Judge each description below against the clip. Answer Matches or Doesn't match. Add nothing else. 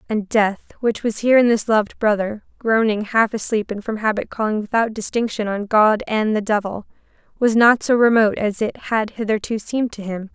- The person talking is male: Doesn't match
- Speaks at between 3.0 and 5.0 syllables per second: Doesn't match